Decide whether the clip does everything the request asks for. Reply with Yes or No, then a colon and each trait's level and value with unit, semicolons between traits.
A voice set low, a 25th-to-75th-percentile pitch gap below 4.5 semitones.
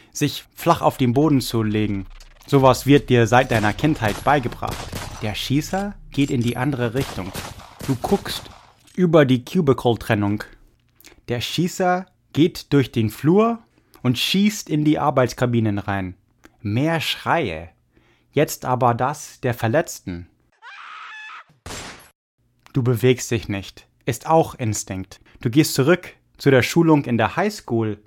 No: low, 125 Hz; wide, 5.5 semitones